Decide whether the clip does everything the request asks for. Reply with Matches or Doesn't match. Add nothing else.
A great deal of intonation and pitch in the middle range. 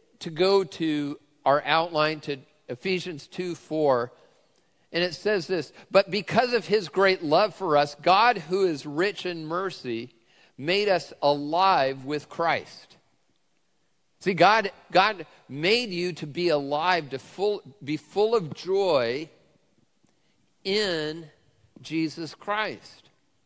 Doesn't match